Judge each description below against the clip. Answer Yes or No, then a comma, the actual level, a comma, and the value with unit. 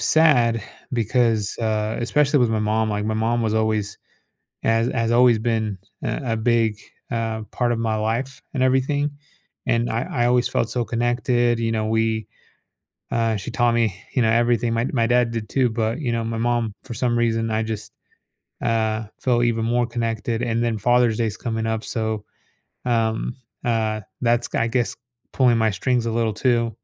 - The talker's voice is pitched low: Yes, low, 115 Hz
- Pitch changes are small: Yes, narrow, 1.4 semitones